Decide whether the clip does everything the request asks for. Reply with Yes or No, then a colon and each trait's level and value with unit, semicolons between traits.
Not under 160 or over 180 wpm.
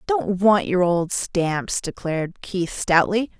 No: average, 140 wpm